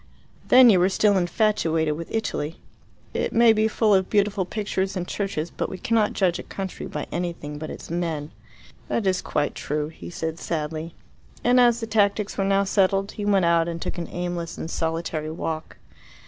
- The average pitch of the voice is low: No, medium, 185 Hz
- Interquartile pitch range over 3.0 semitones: Yes, average, 3.9 semitones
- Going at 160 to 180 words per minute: No, average, 190 wpm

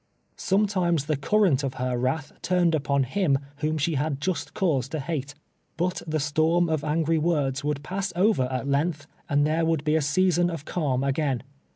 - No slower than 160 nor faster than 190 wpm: Yes, average, 185 wpm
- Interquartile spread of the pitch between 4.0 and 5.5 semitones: No, average, 3.6 semitones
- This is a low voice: No, medium, 155 Hz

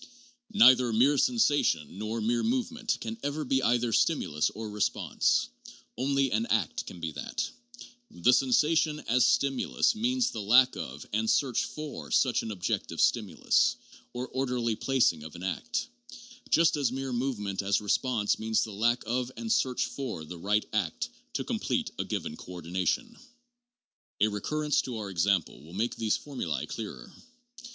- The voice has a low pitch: Yes, low, 120 Hz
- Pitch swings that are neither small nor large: Yes, average, 5.0 semitones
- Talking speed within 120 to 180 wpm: Yes, average, 155 wpm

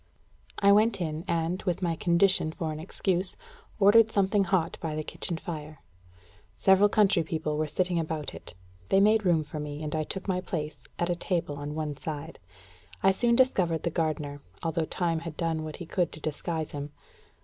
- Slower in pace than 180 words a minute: No, average, 190 wpm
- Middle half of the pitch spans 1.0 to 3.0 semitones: No, average, 3.4 semitones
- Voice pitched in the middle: Yes, medium, 165 Hz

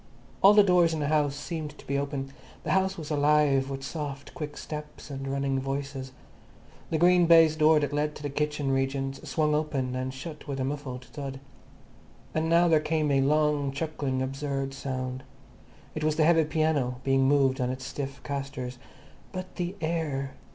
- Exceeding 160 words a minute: Yes, average, 180 wpm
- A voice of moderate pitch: Yes, medium, 145 Hz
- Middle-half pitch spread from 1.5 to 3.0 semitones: Yes, narrow, 2.4 semitones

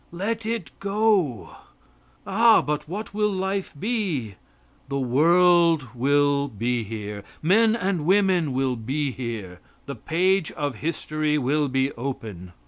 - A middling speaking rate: No, slow, 130 wpm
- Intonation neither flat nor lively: No, wide, 6.9 semitones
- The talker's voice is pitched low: No, medium, 150 Hz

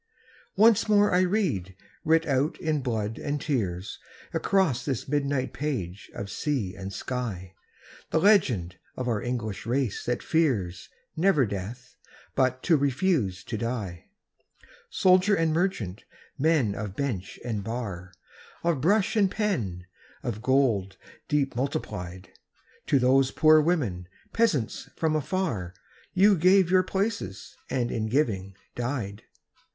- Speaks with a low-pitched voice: Yes, low, 130 Hz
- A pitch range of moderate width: No, wide, 8.0 semitones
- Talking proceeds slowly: Yes, slow, 130 wpm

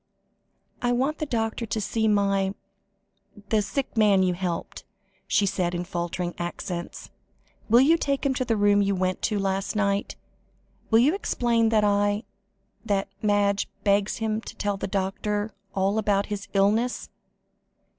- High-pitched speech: Yes, high, 205 Hz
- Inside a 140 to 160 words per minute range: Yes, average, 155 wpm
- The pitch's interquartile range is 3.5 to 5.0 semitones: No, narrow, 2.4 semitones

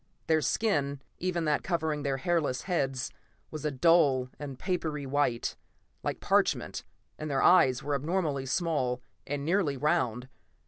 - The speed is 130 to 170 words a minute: Yes, average, 140 wpm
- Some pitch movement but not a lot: Yes, average, 3.7 semitones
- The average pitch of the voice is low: No, medium, 145 Hz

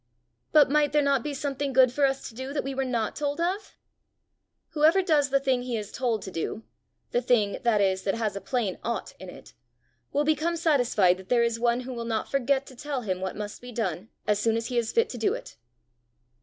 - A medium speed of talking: No, fast, 235 wpm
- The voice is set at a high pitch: Yes, high, 245 Hz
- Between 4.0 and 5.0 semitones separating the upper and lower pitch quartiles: Yes, average, 4.3 semitones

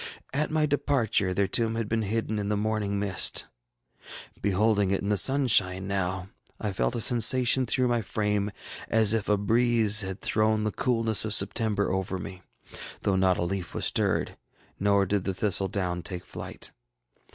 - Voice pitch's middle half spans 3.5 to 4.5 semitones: No, average, 2.7 semitones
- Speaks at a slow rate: No, average, 175 wpm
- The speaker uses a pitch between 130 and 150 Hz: No, low, 105 Hz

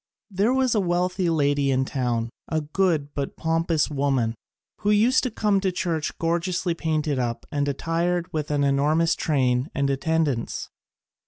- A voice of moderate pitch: Yes, medium, 160 Hz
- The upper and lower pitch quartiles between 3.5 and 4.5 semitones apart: Yes, average, 4.1 semitones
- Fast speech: No, average, 160 wpm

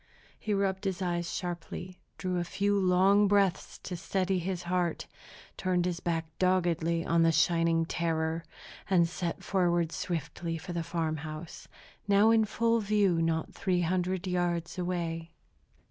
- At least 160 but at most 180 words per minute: No, average, 145 wpm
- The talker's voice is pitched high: No, medium, 175 Hz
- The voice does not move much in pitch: Yes, narrow, 2.1 semitones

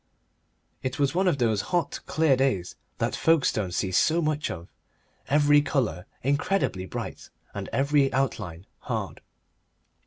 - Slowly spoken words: Yes, slow, 130 wpm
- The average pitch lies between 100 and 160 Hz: Yes, low, 135 Hz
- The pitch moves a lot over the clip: Yes, wide, 6.7 semitones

